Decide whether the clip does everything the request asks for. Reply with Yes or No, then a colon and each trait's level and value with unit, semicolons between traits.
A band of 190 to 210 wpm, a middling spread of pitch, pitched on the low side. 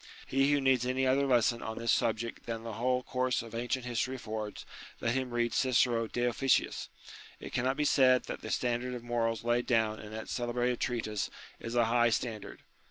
No: average, 195 wpm; narrow, 1.8 semitones; low, 120 Hz